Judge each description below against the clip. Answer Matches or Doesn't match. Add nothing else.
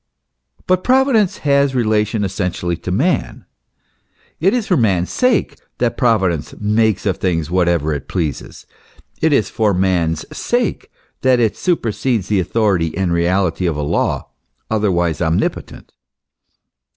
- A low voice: Matches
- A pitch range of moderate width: Doesn't match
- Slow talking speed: Matches